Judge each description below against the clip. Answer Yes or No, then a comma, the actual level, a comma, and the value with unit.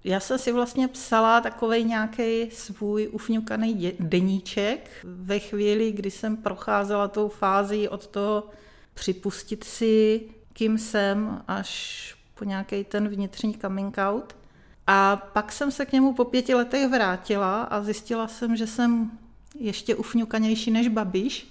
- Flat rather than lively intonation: Yes, narrow, 2.3 semitones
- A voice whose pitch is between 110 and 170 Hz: No, high, 215 Hz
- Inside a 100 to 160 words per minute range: Yes, average, 135 wpm